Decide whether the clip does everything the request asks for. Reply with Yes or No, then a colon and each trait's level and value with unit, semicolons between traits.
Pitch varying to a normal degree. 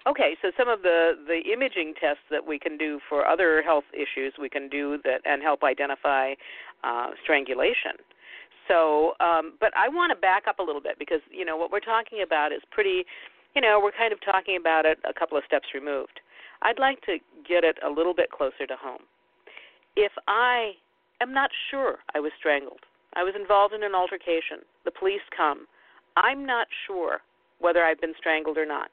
No: wide, 7.8 semitones